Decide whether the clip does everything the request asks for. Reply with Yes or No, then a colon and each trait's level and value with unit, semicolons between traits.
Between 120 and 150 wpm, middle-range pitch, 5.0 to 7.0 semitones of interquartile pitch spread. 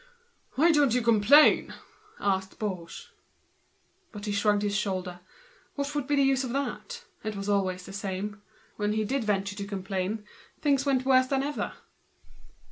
No: average, 145 wpm; high, 210 Hz; average, 5.3 semitones